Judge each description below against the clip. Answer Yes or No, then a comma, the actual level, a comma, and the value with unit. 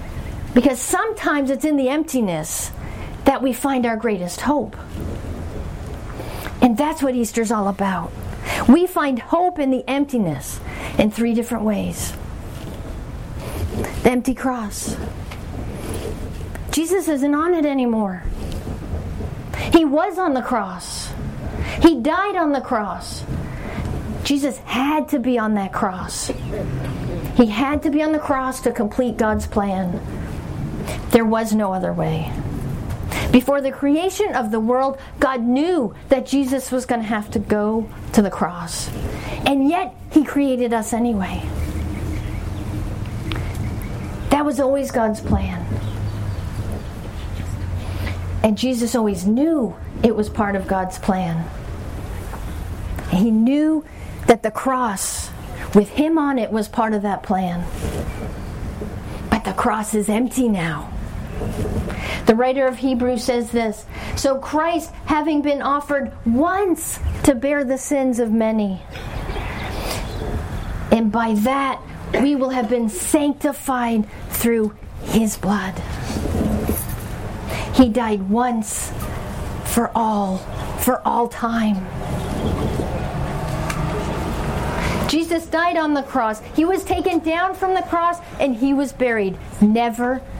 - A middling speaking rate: No, slow, 120 wpm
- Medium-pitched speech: No, high, 235 Hz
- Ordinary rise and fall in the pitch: No, wide, 8.0 semitones